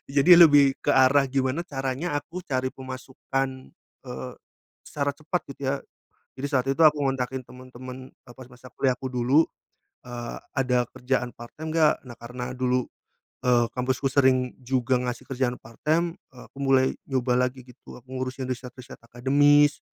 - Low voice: Yes, low, 130 Hz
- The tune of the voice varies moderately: No, narrow, 1.8 semitones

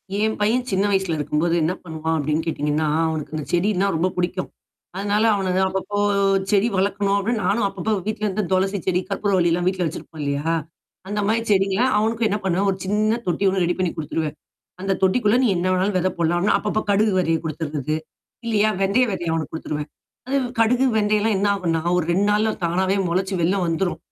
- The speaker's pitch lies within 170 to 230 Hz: Yes, high, 190 Hz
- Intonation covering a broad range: No, average, 3.8 semitones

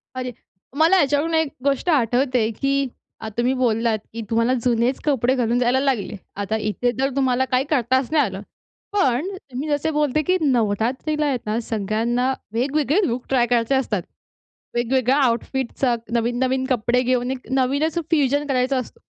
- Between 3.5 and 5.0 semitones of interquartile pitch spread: No, average, 2.7 semitones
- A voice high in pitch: Yes, very high, 255 Hz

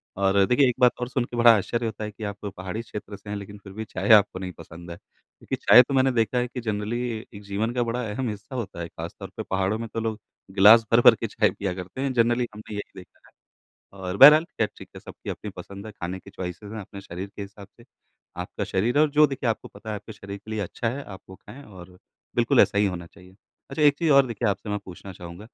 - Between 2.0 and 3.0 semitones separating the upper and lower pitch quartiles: No, average, 3.6 semitones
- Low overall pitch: Yes, low, 105 Hz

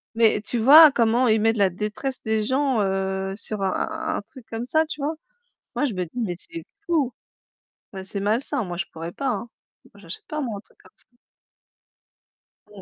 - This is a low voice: No, high, 225 Hz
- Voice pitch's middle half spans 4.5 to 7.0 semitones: Yes, wide, 5.6 semitones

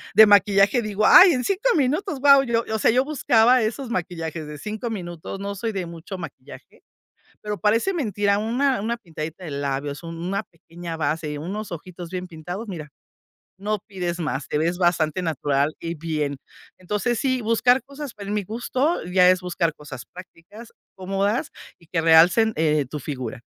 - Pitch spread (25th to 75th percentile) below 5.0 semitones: No, wide, 5.5 semitones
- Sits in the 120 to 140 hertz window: No, medium, 185 Hz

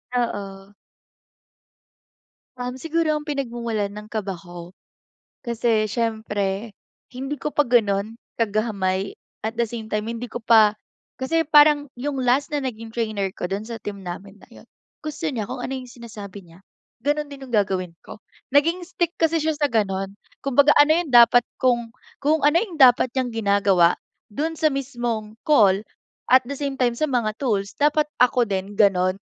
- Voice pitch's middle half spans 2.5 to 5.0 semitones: No, wide, 5.5 semitones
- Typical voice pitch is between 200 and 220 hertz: No, high, 235 Hz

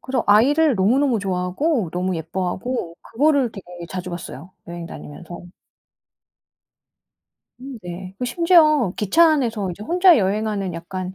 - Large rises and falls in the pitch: Yes, wide, 6.9 semitones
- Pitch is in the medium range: No, high, 205 Hz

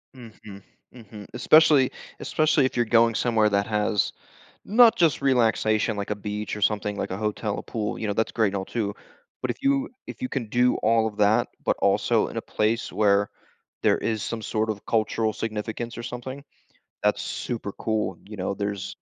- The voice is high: No, low, 110 Hz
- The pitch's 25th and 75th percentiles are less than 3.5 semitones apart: Yes, narrow, 2.5 semitones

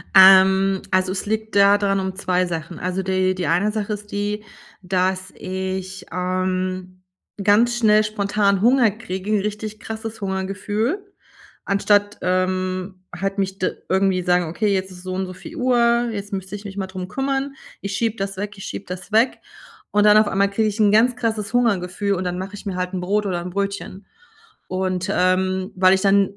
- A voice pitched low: No, high, 195 Hz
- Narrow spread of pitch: Yes, narrow, 2.1 semitones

